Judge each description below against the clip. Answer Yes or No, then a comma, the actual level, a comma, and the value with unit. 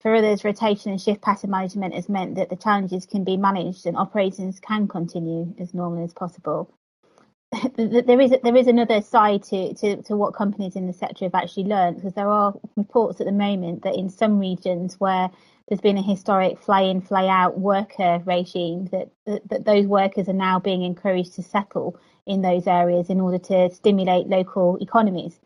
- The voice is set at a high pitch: Yes, high, 195 Hz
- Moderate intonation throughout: No, narrow, 2.2 semitones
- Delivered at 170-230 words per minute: Yes, average, 185 wpm